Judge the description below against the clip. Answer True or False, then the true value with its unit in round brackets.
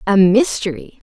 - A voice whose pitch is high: True (205 Hz)